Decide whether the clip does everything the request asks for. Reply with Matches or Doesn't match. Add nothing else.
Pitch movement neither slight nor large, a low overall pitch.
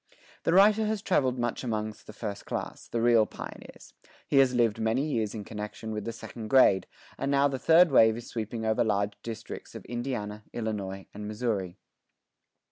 Matches